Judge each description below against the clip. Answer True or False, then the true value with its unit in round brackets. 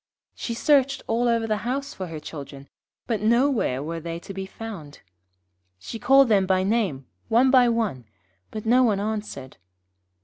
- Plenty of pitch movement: True (6.0 semitones)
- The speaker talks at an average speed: True (165 wpm)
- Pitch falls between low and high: False (215 Hz)